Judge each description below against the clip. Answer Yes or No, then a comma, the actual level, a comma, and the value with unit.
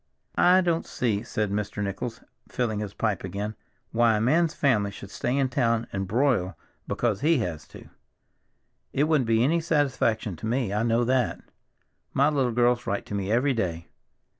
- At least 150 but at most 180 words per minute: Yes, average, 175 wpm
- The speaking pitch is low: Yes, low, 115 Hz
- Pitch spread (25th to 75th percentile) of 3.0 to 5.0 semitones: Yes, average, 4.6 semitones